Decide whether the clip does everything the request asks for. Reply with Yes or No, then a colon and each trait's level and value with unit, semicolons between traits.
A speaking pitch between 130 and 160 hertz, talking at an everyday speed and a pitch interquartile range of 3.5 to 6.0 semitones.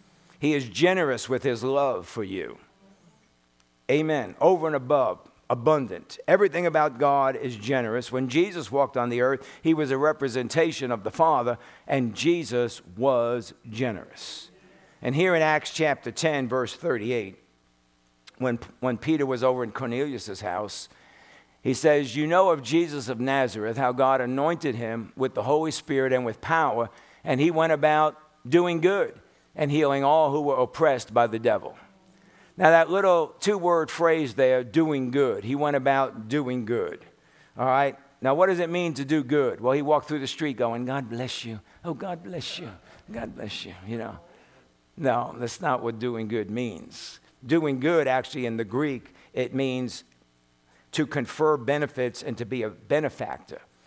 Yes: low, 135 Hz; average, 170 wpm; average, 4.3 semitones